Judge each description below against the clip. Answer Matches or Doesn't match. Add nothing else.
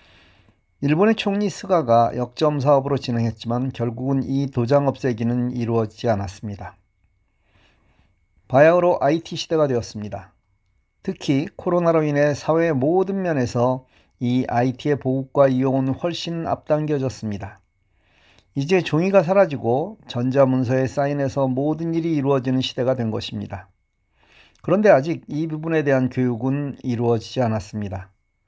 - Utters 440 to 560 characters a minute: Doesn't match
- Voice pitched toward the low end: Matches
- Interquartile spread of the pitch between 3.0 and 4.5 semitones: Doesn't match